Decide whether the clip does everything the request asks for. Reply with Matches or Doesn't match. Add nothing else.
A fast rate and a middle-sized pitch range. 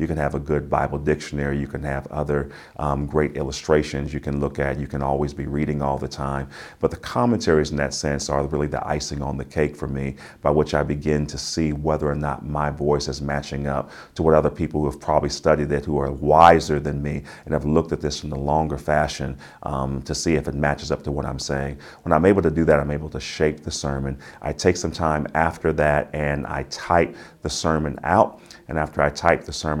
Doesn't match